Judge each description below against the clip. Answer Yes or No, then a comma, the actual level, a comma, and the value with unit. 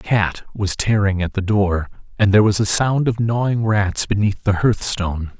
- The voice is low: Yes, low, 100 Hz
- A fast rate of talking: Yes, fast, 210 wpm